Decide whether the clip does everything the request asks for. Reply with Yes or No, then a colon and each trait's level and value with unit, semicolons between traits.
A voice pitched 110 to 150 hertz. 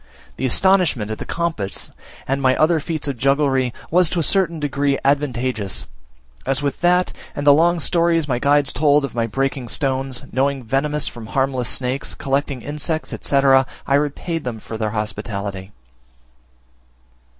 Yes: medium, 140 Hz